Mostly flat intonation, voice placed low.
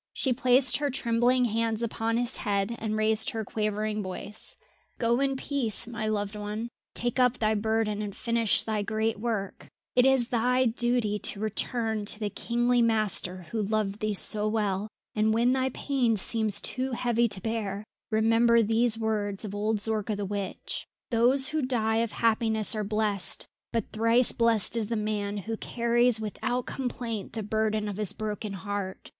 No: narrow, 2.1 semitones; high, 220 Hz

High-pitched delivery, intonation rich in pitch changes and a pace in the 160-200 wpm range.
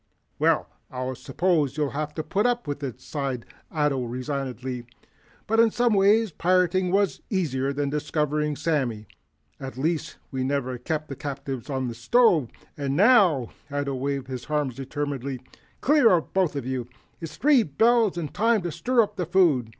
No: medium, 145 Hz; wide, 5.8 semitones; average, 170 wpm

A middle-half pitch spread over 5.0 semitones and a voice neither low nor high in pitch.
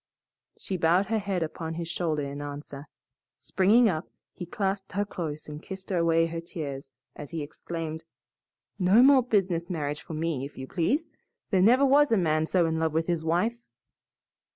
No: average, 3.8 semitones; medium, 170 Hz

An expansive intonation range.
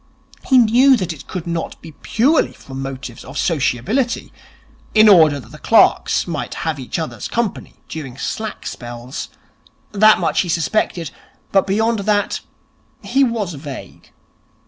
Yes: wide, 7.5 semitones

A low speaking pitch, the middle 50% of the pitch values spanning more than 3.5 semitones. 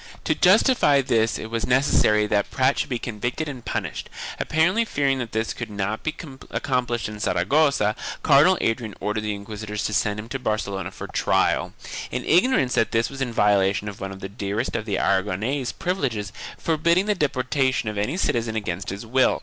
Yes: low, 115 Hz; average, 4.7 semitones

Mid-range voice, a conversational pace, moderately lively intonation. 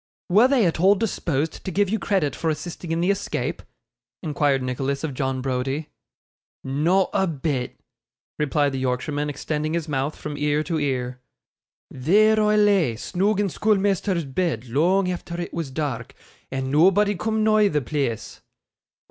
No: medium, 155 Hz; average, 155 wpm; wide, 5.9 semitones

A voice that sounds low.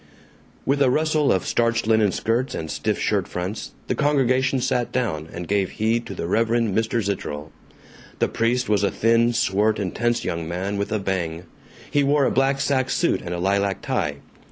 Yes: low, 110 Hz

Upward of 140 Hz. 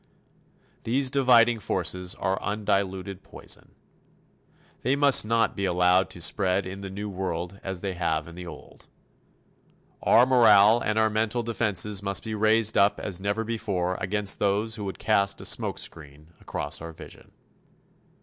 No: low, 100 Hz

